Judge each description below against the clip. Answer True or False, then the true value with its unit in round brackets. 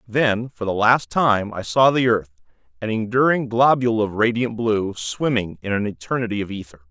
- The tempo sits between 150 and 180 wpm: True (175 wpm)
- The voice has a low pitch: True (110 Hz)